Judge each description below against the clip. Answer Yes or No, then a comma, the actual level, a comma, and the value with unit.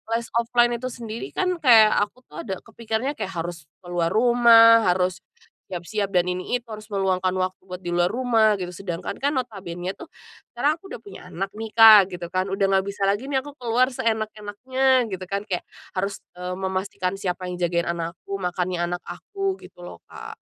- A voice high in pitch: Yes, high, 200 Hz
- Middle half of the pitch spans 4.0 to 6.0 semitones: Yes, average, 4.3 semitones